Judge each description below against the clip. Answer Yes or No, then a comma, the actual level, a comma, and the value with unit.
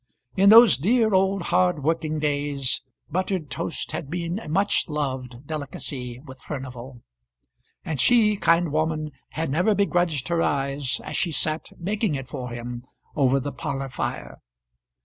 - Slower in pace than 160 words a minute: Yes, average, 150 wpm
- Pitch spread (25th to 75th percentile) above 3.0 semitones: Yes, average, 4.8 semitones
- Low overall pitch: No, medium, 155 Hz